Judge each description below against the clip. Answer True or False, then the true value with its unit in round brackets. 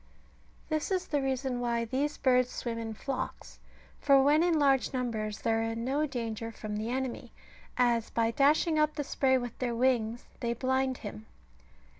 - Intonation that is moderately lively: True (3.1 semitones)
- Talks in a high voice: True (250 Hz)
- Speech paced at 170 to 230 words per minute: True (175 wpm)